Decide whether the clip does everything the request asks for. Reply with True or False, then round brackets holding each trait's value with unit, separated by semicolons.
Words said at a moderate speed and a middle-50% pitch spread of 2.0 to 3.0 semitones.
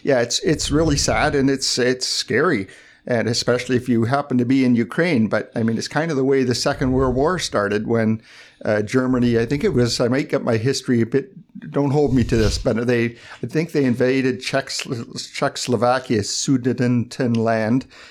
True (195 wpm; 2.6 semitones)